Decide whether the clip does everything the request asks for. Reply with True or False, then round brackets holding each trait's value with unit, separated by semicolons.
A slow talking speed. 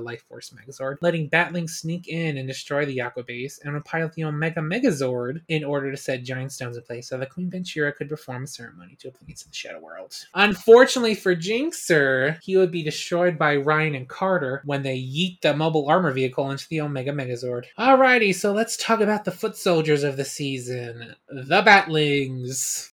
False (195 wpm)